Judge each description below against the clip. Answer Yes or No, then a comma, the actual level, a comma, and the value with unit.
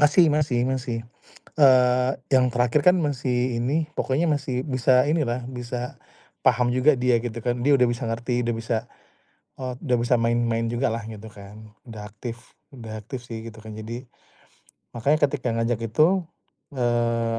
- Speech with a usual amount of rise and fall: No, narrow, 2.2 semitones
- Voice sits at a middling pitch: No, low, 125 Hz